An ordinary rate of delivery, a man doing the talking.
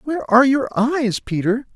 Yes: average, 170 wpm; male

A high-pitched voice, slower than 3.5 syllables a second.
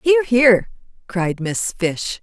Yes: high, 210 Hz; 2.8 syllables/s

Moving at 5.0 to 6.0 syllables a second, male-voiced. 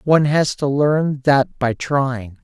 No: 3.5 syllables/s; male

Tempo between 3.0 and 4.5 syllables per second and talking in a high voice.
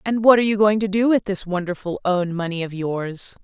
No: 5.5 syllables/s; high, 195 Hz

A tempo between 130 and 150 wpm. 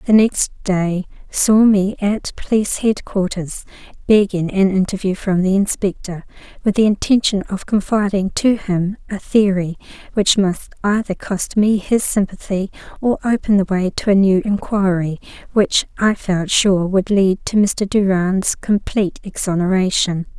Yes: average, 145 wpm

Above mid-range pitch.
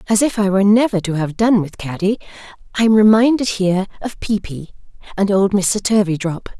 Yes: high, 200 Hz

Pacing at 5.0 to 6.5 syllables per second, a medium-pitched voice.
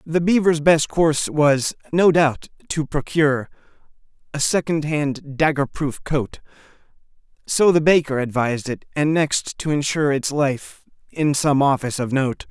No: 4.5 syllables/s; medium, 145 Hz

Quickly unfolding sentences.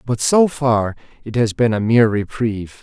No: average, 190 wpm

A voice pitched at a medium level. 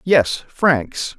Yes: medium, 145 Hz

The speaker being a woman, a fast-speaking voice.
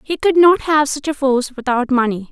Yes: female; fast, 235 wpm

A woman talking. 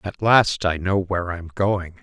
No: male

